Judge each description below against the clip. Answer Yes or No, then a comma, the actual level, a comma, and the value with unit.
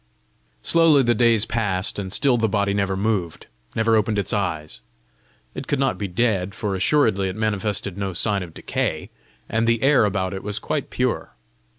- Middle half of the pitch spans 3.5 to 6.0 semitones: No, average, 2.9 semitones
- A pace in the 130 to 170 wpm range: No, average, 180 wpm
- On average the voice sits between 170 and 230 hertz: No, low, 105 Hz